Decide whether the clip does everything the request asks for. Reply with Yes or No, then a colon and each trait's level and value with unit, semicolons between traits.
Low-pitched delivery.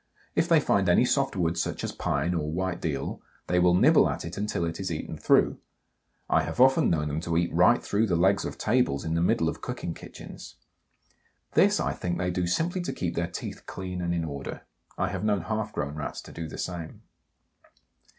Yes: very low, 90 Hz